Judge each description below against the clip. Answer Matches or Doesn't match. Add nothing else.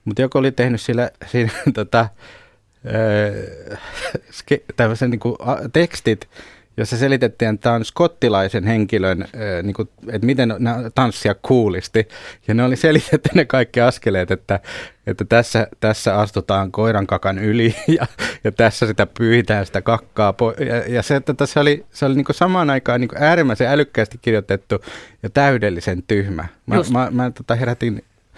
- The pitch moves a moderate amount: Matches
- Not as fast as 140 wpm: Doesn't match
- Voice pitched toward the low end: Matches